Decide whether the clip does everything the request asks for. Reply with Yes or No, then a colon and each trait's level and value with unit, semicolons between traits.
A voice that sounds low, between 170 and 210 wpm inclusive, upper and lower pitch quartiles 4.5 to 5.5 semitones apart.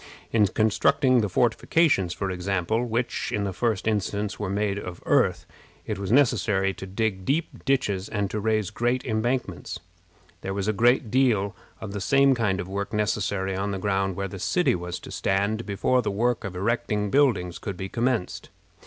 No: low, 105 Hz; average, 180 wpm; average, 3.5 semitones